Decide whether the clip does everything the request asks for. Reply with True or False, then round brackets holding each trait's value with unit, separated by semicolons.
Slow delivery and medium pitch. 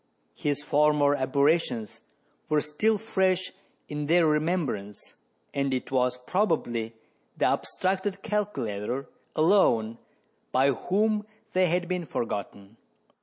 True (105 wpm; 150 Hz)